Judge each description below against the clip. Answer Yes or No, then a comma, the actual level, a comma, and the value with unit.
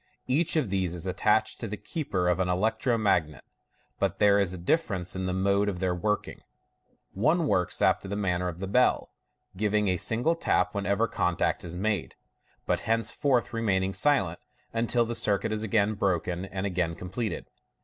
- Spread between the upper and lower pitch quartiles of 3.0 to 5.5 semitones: Yes, average, 3.8 semitones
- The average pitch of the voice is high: No, low, 100 Hz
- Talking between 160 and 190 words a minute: Yes, average, 180 wpm